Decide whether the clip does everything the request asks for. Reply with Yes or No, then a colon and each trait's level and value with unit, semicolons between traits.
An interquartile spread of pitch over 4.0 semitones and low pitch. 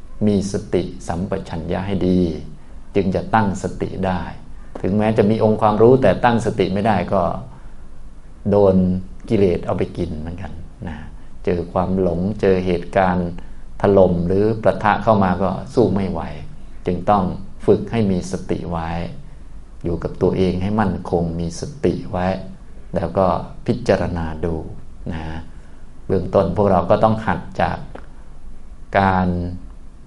No: average, 3.0 semitones; very low, 90 Hz